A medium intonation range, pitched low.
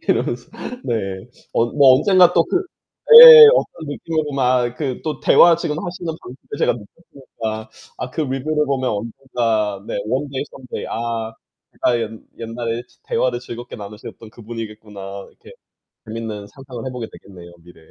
Yes: average, 4.6 semitones; low, 125 Hz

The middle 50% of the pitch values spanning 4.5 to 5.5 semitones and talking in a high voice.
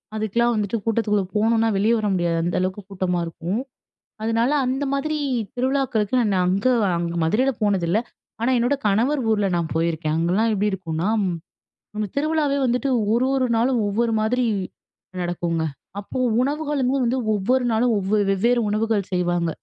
Yes: average, 4.9 semitones; high, 215 Hz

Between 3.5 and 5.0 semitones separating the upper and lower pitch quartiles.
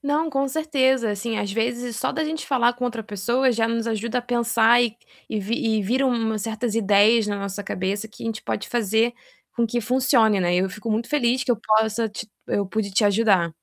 No: average, 2.7 semitones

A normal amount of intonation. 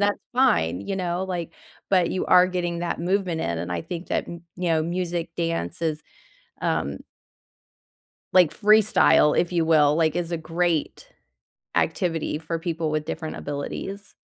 No: narrow, 2.3 semitones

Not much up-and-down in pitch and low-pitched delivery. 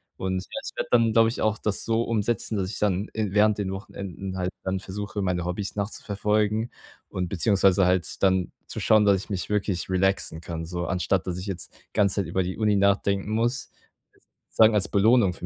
Yes: narrow, 2.3 semitones; low, 100 Hz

